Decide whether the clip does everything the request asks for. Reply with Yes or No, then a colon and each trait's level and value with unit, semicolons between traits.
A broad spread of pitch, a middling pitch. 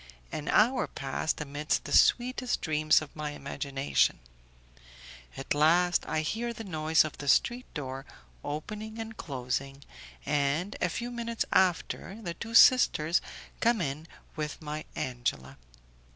Yes: wide, 7.4 semitones; medium, 155 Hz